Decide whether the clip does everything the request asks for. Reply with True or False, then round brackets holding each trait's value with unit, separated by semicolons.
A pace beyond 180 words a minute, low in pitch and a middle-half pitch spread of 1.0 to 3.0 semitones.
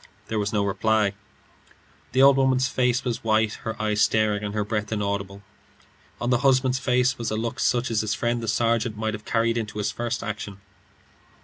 True (195 wpm; 110 Hz; 2.4 semitones)